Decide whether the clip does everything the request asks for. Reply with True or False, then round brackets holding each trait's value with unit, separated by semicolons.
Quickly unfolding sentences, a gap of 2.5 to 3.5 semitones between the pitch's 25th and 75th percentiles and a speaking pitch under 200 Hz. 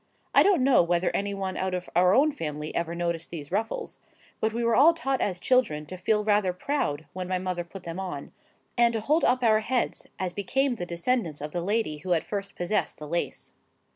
False (215 wpm; 5.3 semitones; 190 Hz)